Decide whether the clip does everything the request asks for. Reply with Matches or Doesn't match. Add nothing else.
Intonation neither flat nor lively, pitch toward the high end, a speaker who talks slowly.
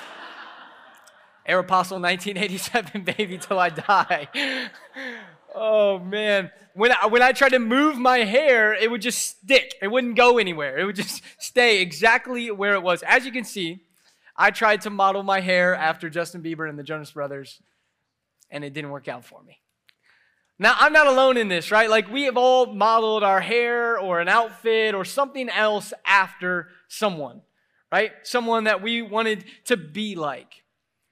Doesn't match